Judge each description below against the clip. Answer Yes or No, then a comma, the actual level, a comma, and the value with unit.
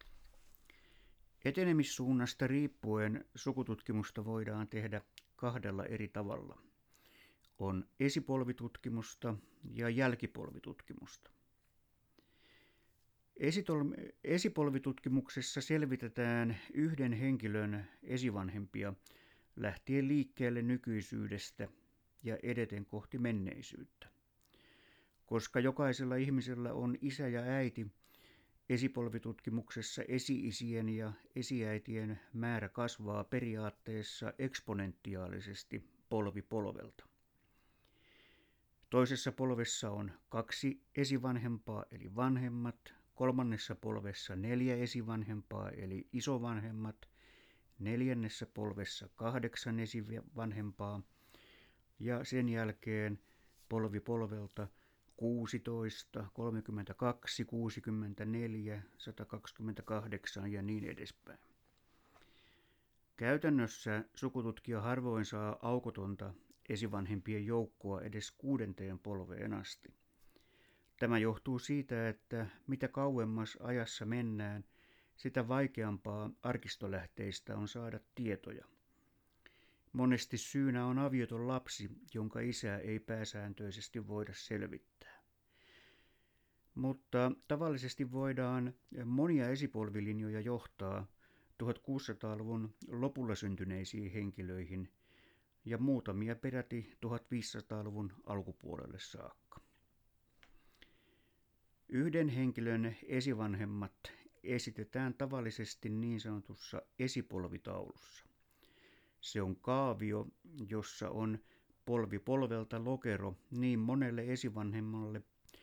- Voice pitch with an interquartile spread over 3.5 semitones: No, average, 3.1 semitones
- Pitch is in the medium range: No, low, 115 Hz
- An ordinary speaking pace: No, slow, 75 wpm